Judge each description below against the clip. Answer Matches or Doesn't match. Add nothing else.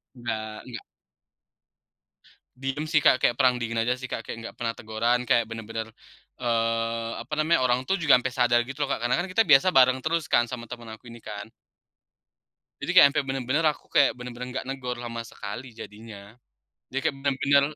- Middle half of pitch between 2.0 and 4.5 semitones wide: Matches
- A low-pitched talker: Matches